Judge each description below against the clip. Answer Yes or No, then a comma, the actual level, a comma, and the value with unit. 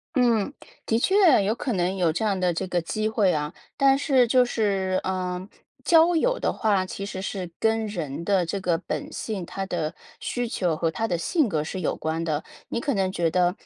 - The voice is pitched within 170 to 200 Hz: Yes, high, 195 Hz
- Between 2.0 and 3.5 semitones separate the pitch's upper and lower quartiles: No, average, 4.3 semitones